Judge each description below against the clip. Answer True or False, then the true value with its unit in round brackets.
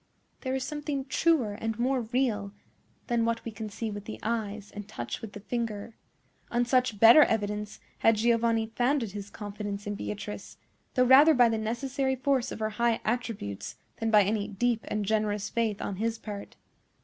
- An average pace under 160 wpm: False (180 wpm)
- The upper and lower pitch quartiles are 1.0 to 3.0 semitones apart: True (2.7 semitones)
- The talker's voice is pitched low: False (225 Hz)